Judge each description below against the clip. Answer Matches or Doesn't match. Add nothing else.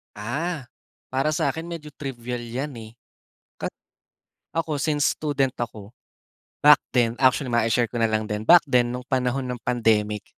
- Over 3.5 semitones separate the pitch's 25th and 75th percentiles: Matches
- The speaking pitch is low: Matches